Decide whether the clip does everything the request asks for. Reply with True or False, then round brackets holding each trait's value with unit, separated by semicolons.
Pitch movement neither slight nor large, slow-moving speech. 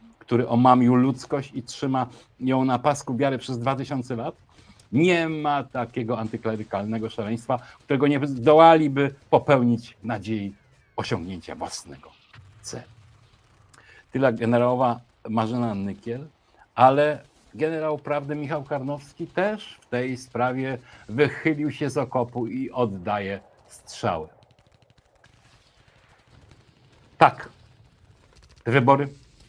True (3.5 semitones; 95 wpm)